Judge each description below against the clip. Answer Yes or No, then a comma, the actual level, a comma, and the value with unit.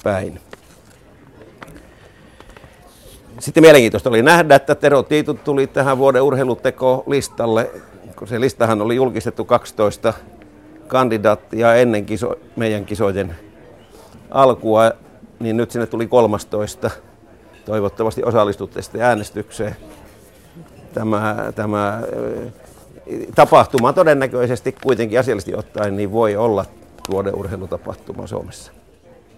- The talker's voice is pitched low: Yes, low, 115 Hz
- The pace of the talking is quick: No, slow, 95 wpm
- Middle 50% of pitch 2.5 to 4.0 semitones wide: Yes, average, 3.6 semitones